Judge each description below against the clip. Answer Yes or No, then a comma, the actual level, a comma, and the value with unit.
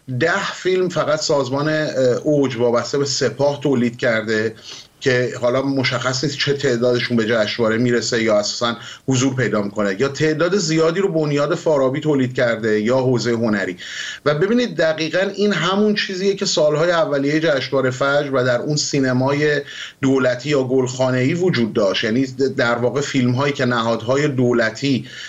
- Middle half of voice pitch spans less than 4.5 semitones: Yes, average, 3.7 semitones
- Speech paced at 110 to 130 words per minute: No, average, 145 wpm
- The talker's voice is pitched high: No, low, 135 Hz